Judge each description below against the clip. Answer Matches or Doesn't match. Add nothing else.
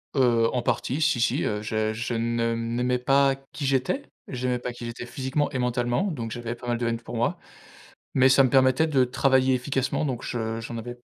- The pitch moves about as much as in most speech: Doesn't match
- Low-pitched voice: Matches